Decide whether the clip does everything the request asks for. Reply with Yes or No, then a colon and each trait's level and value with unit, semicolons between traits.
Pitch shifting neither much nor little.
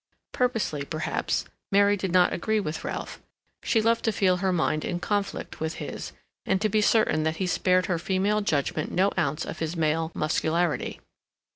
Yes: average, 4.2 semitones